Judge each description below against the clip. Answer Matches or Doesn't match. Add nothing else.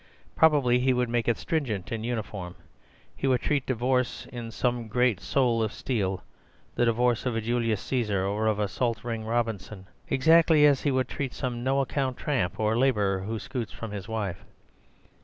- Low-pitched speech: Matches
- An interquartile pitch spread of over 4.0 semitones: Doesn't match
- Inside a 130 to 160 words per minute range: Doesn't match